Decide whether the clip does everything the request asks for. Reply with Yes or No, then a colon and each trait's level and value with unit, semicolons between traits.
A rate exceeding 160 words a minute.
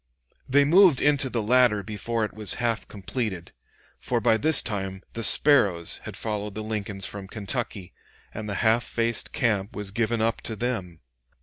Yes: average, 170 wpm